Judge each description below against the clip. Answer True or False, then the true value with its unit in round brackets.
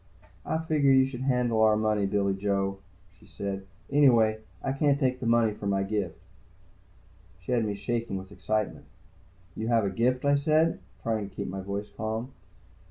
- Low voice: True (110 Hz)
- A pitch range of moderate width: True (4.1 semitones)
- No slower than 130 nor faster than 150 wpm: False (165 wpm)